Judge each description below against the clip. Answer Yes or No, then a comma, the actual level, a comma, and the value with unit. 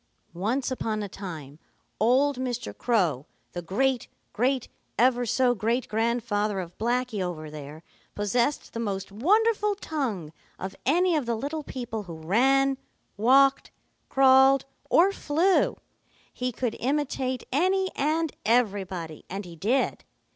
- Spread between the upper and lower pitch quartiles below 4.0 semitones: No, average, 5.3 semitones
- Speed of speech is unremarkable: No, slow, 130 wpm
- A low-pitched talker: No, high, 245 Hz